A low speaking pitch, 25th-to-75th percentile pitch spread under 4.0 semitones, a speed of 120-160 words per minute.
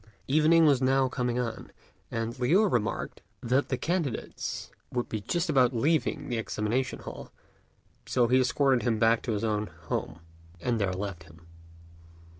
Yes: low, 125 Hz; average, 3.3 semitones; average, 155 wpm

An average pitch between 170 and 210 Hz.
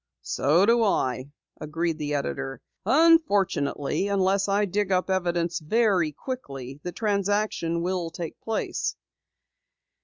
Yes: medium, 185 Hz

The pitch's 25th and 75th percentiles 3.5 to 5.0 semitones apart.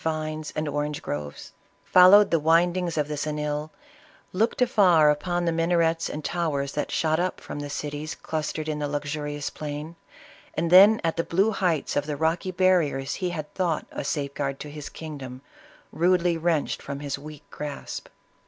No: average, 2.8 semitones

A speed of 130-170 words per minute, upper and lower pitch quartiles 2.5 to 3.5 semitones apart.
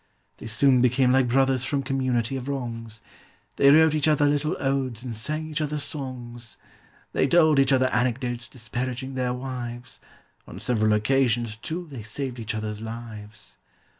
Yes: average, 160 wpm; average, 2.8 semitones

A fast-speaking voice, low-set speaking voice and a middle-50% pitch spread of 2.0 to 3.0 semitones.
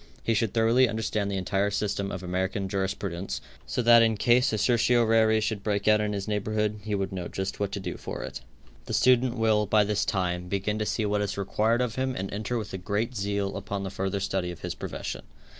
Yes: fast, 220 wpm; low, 105 Hz; narrow, 2.4 semitones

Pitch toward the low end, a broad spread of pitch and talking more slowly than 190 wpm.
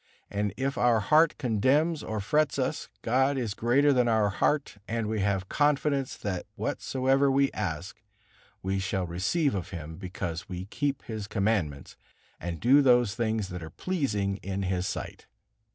Yes: low, 110 Hz; wide, 5.9 semitones; average, 160 wpm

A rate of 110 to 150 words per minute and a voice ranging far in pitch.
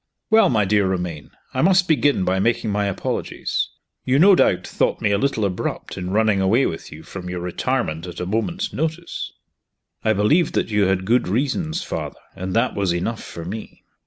No: average, 190 wpm; wide, 6.6 semitones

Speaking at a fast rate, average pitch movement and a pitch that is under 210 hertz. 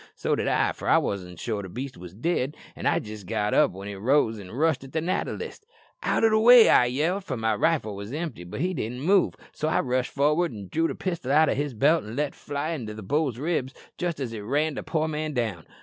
No: fast, 260 wpm; wide, 6.6 semitones; low, 135 Hz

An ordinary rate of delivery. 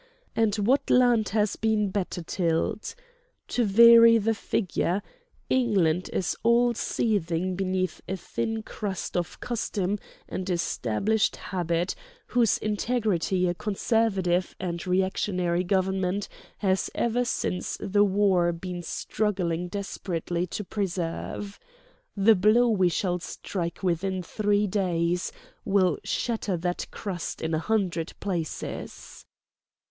No: slow, 115 wpm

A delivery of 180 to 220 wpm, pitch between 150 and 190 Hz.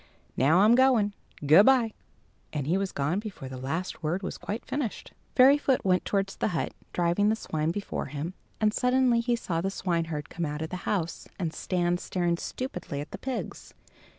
Yes: average, 185 wpm; medium, 185 Hz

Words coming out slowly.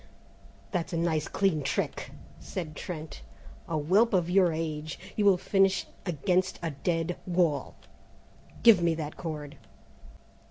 Yes: slow, 125 wpm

